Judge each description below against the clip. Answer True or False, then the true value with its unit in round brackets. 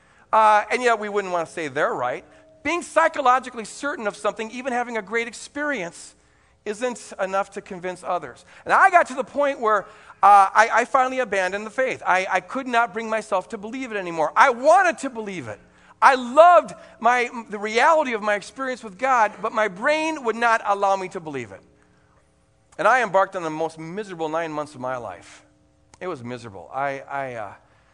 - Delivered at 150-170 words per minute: False (200 wpm)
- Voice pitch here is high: True (215 Hz)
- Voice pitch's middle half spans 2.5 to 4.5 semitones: False (5.6 semitones)